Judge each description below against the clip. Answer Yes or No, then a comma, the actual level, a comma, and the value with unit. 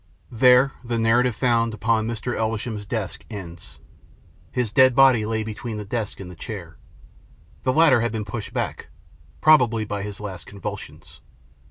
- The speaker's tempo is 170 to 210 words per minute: No, average, 155 wpm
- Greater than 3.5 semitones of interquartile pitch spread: No, average, 2.7 semitones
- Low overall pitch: Yes, low, 110 Hz